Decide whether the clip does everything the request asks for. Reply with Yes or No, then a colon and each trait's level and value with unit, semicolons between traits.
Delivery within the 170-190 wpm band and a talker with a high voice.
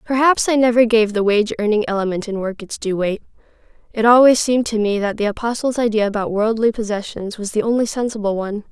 No: fast, 205 wpm; high, 220 Hz